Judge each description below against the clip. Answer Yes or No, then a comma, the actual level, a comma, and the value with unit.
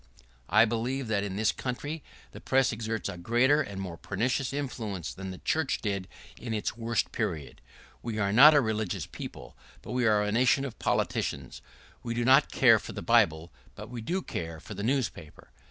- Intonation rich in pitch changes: No, average, 4.4 semitones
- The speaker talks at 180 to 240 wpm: Yes, average, 195 wpm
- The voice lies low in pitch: Yes, low, 115 Hz